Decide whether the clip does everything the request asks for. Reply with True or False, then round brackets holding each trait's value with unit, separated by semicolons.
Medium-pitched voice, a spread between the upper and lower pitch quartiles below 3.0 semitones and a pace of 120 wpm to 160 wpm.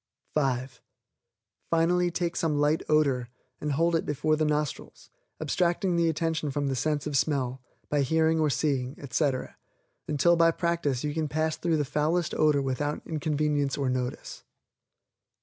True (150 Hz; 2.6 semitones; 150 wpm)